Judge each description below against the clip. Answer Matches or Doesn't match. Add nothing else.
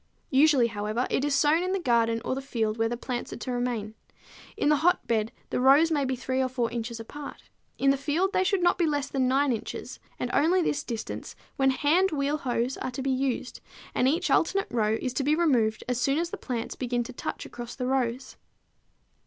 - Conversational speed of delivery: Doesn't match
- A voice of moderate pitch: Doesn't match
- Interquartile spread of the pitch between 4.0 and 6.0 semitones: Doesn't match